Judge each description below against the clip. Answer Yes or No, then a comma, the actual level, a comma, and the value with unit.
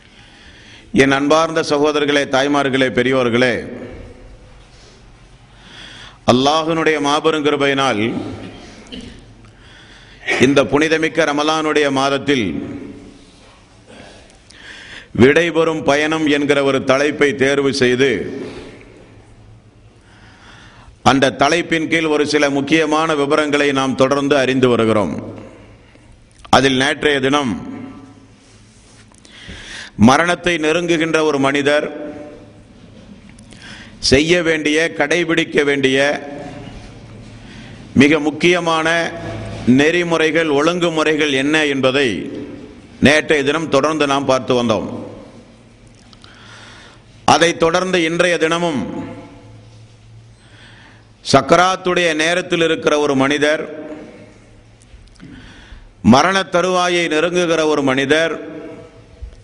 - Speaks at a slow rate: Yes, slow, 70 wpm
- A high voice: No, medium, 140 Hz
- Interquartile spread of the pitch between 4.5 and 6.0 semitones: Yes, average, 5.2 semitones